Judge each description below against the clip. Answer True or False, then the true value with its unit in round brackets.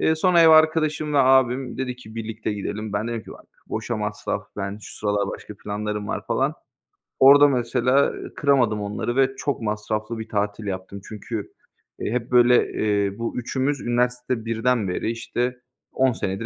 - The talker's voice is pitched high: False (115 Hz)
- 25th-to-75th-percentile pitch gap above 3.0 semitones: True (3.6 semitones)